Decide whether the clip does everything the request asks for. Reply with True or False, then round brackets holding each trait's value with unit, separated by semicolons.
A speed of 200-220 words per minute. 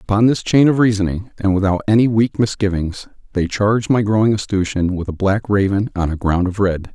True (205 wpm)